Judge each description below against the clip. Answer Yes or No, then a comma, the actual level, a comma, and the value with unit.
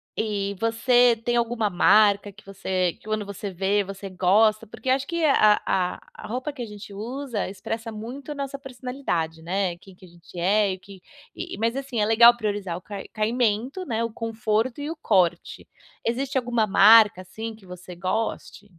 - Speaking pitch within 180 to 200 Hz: No, high, 215 Hz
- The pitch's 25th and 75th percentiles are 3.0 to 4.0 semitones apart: Yes, average, 3.6 semitones